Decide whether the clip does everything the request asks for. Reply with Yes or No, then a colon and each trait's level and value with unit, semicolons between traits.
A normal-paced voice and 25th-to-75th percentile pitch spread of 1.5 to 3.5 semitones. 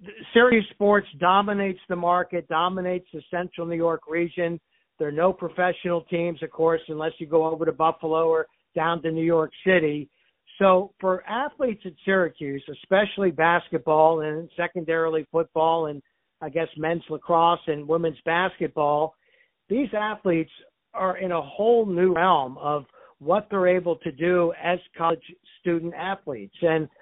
Yes: average, 150 wpm; narrow, 2.4 semitones